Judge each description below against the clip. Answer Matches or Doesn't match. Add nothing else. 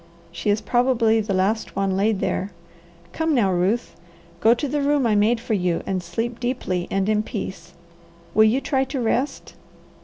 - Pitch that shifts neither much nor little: Matches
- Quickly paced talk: Doesn't match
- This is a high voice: Matches